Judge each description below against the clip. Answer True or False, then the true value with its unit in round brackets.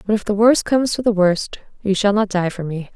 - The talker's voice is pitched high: True (200 Hz)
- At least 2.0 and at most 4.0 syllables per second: False (5.8 syllables/s)